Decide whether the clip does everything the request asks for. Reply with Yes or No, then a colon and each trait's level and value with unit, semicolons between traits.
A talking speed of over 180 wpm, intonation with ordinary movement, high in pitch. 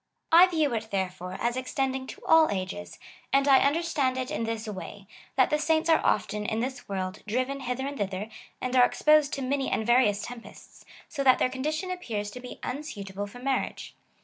Yes: average, 195 wpm; average, 4.9 semitones; very high, 255 Hz